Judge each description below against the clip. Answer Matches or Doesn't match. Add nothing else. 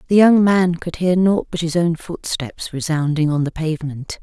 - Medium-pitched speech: Matches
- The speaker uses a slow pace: Doesn't match